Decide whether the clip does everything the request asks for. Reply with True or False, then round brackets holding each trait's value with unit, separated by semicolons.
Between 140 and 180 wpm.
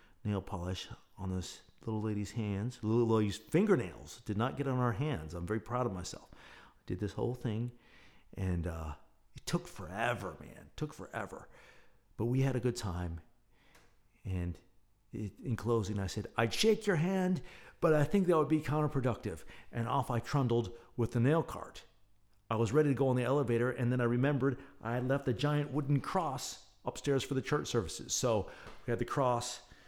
False (190 wpm)